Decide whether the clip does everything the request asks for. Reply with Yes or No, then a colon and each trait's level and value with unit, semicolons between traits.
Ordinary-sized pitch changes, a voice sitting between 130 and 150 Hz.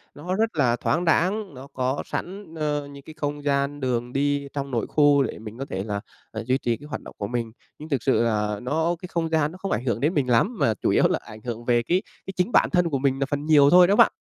Yes: average, 4.8 semitones; medium, 140 Hz